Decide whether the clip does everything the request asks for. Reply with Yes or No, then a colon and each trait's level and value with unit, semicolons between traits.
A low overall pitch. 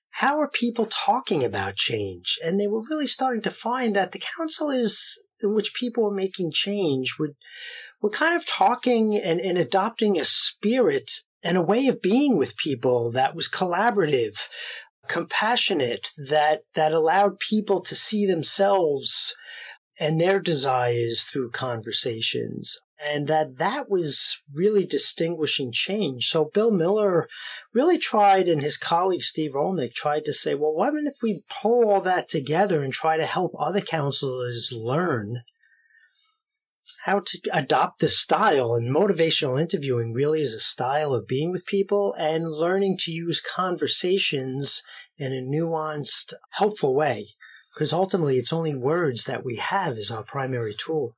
No: medium, 180 Hz